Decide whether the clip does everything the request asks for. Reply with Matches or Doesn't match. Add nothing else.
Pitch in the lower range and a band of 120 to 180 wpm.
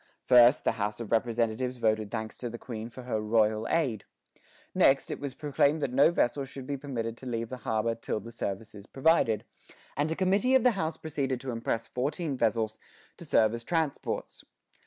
Doesn't match